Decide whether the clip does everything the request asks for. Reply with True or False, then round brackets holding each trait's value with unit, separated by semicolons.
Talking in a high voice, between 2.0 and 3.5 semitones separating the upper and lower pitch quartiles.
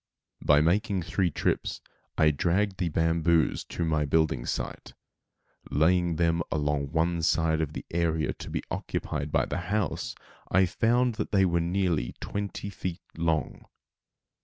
False (85 Hz; 2.7 semitones)